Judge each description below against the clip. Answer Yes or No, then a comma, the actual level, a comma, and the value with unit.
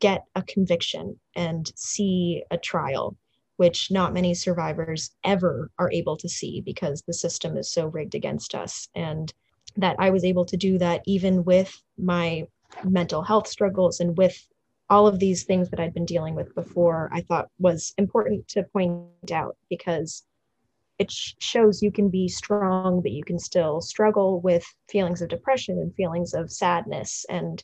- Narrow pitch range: Yes, narrow, 2.0 semitones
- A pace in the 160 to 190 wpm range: Yes, average, 170 wpm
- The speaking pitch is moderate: Yes, medium, 180 Hz